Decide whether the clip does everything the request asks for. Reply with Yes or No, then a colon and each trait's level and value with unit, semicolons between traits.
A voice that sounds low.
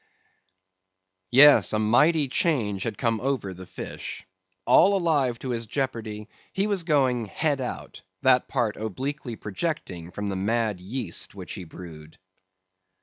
Yes: low, 120 Hz